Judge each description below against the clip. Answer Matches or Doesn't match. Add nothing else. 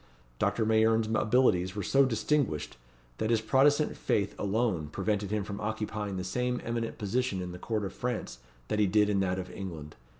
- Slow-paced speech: Doesn't match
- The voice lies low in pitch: Matches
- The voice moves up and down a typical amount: Matches